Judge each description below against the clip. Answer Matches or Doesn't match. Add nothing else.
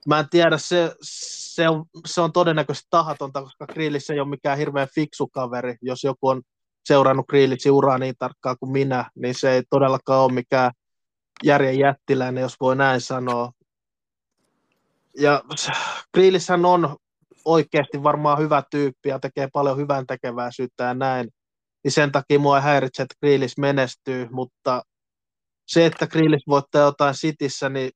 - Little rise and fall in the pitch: Matches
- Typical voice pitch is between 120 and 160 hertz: Matches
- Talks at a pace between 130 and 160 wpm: Matches